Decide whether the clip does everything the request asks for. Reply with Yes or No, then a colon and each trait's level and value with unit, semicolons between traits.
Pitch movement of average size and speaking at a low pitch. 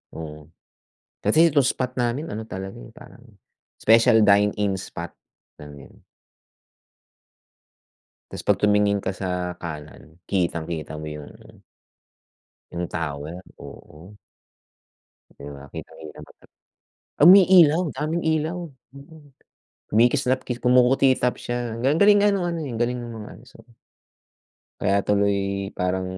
No: wide, 6.7 semitones; low, 105 Hz